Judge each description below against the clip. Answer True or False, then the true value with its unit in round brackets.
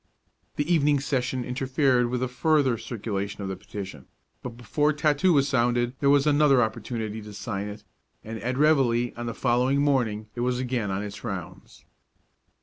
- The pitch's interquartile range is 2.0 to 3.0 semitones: False (4.1 semitones)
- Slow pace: False (170 wpm)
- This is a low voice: True (125 Hz)